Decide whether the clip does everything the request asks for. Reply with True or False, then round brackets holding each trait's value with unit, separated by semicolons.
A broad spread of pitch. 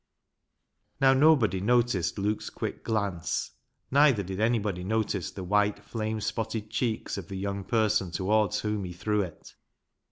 False (2.6 semitones)